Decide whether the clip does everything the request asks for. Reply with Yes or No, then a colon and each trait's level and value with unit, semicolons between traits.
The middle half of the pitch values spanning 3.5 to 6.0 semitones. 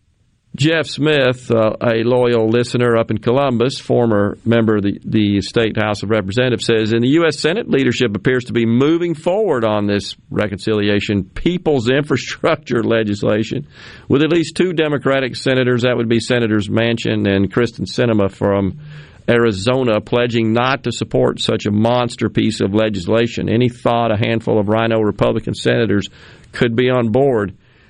No: average, 2.7 semitones